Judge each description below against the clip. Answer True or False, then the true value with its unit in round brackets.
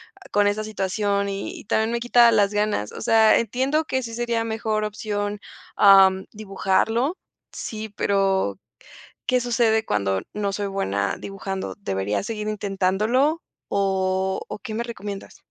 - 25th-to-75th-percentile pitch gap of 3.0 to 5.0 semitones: False (2.6 semitones)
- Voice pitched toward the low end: False (205 Hz)